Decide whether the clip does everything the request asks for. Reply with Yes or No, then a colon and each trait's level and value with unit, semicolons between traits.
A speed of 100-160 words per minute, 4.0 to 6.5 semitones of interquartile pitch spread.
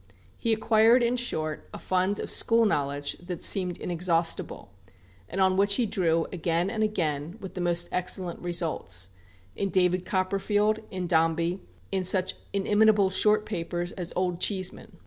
No: average, 150 wpm; average, 2.9 semitones